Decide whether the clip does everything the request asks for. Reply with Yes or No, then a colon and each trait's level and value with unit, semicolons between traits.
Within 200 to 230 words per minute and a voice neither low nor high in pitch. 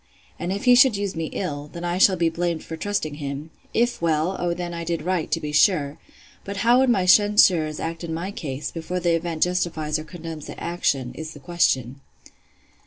Yes: fast, 205 wpm; medium, 170 Hz